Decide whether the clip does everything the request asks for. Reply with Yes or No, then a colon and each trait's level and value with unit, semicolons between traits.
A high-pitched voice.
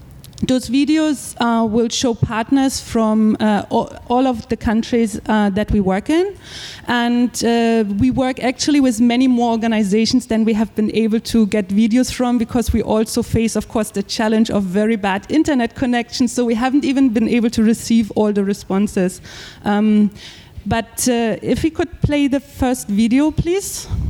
Yes: high, 230 Hz